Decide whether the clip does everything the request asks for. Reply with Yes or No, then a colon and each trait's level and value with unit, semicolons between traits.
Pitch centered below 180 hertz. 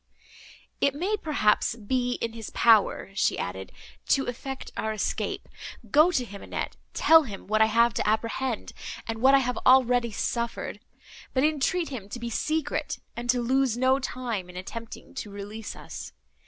No: high, 235 Hz